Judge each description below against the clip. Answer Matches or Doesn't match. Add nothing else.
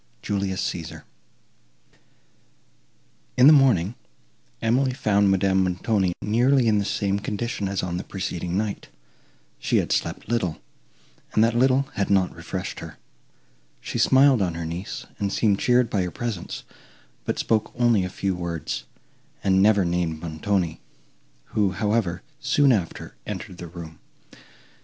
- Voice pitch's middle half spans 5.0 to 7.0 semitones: Doesn't match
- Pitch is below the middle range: Matches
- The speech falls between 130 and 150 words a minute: Matches